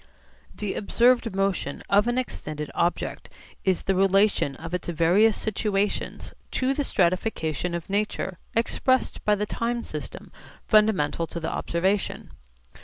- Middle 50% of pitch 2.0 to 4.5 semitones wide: Yes, average, 4.2 semitones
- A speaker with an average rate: No, slow, 130 wpm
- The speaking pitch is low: No, high, 195 Hz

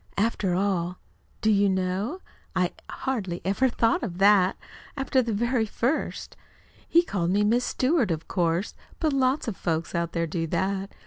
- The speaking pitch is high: Yes, high, 200 Hz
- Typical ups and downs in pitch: Yes, average, 4.9 semitones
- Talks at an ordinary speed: Yes, average, 165 wpm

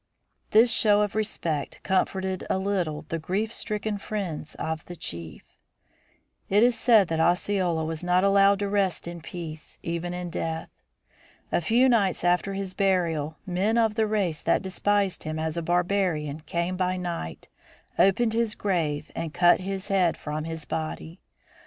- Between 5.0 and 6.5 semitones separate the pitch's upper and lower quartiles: No, average, 3.7 semitones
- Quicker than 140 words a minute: Yes, average, 160 wpm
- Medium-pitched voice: Yes, medium, 180 Hz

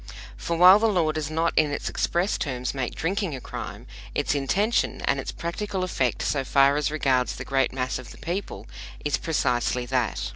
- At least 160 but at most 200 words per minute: Yes, average, 190 wpm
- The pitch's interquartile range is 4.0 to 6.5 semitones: Yes, average, 5.1 semitones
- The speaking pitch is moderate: Yes, medium, 150 Hz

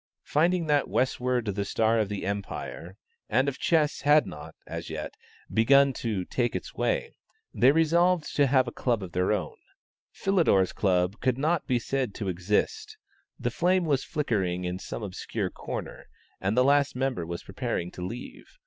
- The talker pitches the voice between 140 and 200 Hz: No, low, 125 Hz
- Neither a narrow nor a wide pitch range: No, wide, 6.8 semitones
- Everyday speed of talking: Yes, average, 165 wpm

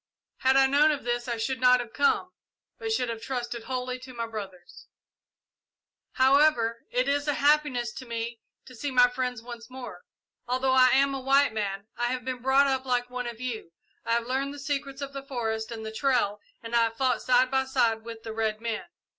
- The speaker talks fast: Yes, fast, 215 wpm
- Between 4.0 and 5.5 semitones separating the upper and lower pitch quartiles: No, narrow, 2.6 semitones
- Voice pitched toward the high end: Yes, very high, 250 Hz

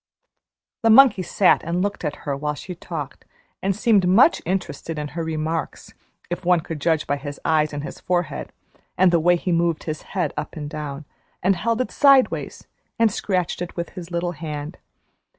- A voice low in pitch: No, medium, 170 Hz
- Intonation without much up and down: No, average, 3.4 semitones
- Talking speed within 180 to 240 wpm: Yes, average, 185 wpm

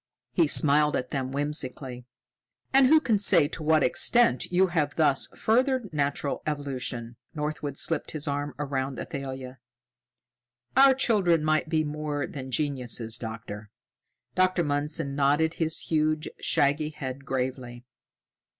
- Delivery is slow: Yes, slow, 130 wpm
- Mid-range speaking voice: Yes, medium, 145 Hz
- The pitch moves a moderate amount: Yes, average, 3.2 semitones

